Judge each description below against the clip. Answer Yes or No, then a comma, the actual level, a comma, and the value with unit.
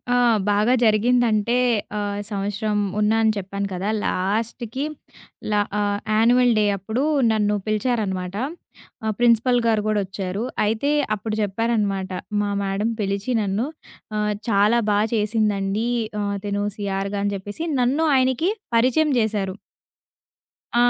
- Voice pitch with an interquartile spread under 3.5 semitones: Yes, narrow, 2.5 semitones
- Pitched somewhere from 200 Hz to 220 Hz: Yes, high, 210 Hz